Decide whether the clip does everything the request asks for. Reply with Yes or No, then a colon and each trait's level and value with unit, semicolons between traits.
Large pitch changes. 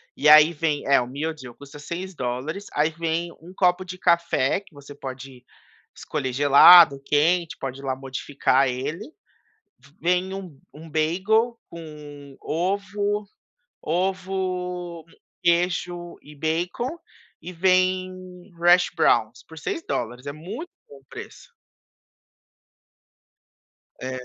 No: average, 4.4 semitones